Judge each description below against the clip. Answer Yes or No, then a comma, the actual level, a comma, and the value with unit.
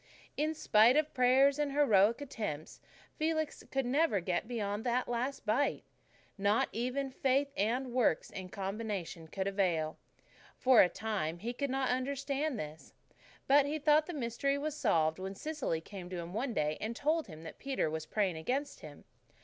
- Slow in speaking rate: No, average, 170 wpm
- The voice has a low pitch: No, high, 235 Hz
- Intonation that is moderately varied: No, wide, 6.6 semitones